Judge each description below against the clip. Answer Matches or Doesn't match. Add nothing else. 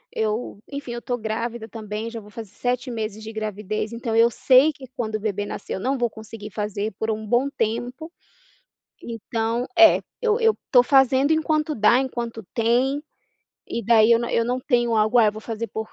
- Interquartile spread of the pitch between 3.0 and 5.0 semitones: Doesn't match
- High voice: Matches